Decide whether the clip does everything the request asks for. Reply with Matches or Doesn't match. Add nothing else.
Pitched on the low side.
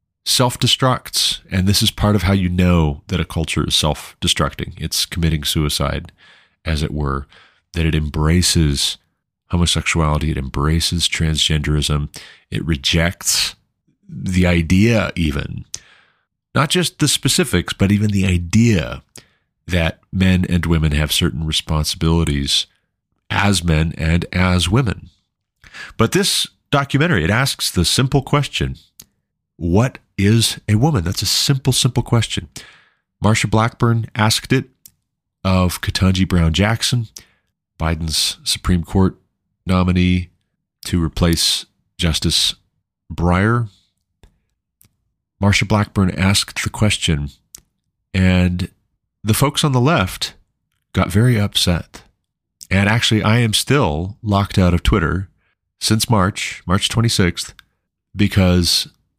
Matches